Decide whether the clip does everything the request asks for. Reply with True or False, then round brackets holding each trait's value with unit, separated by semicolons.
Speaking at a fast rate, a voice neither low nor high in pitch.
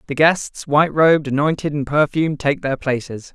False (180 wpm; 145 Hz)